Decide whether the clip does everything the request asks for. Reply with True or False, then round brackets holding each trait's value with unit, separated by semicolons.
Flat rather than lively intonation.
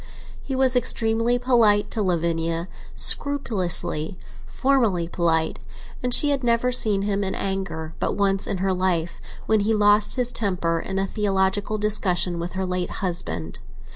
False (4.1 semitones)